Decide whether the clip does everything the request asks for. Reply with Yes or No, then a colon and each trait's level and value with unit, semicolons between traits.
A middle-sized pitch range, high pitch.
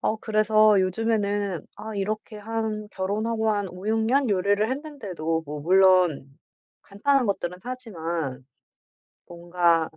Yes: average, 3.9 semitones; high, 205 Hz